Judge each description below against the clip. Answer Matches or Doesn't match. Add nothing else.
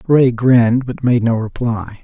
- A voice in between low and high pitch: Doesn't match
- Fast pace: Doesn't match